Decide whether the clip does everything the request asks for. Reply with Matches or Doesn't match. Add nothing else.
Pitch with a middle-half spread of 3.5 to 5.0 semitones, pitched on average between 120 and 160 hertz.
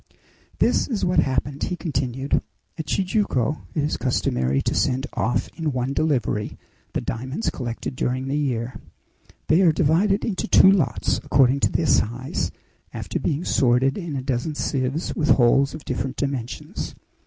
Matches